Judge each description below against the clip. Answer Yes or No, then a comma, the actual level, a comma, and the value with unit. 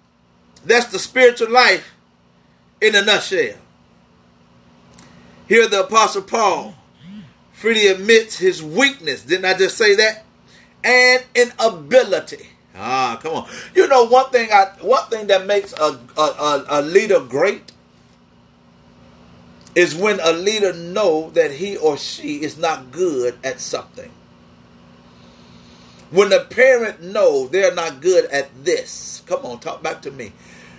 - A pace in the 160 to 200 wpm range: No, slow, 135 wpm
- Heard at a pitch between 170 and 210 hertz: Yes, medium, 185 Hz